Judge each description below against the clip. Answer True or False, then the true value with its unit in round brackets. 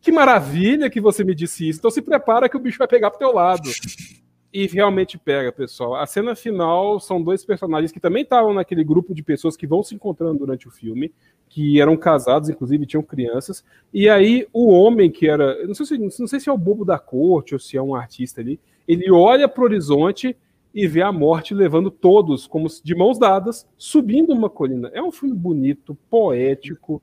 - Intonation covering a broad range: True (6.7 semitones)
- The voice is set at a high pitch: False (180 Hz)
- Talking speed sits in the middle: False (205 wpm)